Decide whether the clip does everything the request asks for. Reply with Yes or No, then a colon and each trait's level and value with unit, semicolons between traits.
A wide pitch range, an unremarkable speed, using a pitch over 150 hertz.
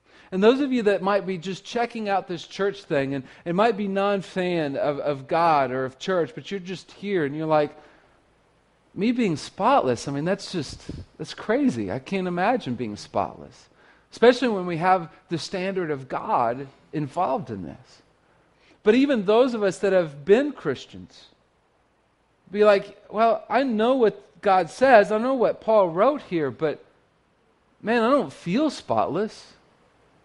Yes: wide, 5.7 semitones; average, 170 wpm; high, 190 Hz